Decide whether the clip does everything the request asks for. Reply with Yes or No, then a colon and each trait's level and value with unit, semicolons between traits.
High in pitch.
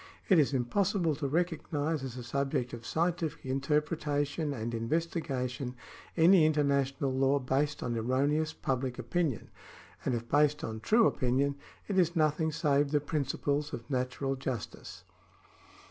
No: medium, 140 Hz